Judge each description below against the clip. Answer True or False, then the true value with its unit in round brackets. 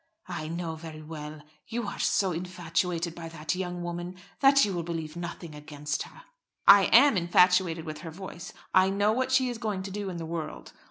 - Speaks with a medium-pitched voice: True (175 Hz)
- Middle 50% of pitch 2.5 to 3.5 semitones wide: True (3.1 semitones)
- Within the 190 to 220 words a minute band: True (200 wpm)